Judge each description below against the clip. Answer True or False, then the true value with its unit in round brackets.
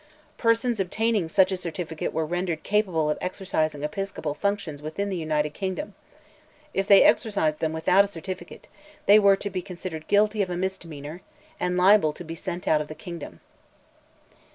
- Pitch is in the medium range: True (180 Hz)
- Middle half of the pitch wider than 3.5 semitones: True (4.0 semitones)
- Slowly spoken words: False (170 wpm)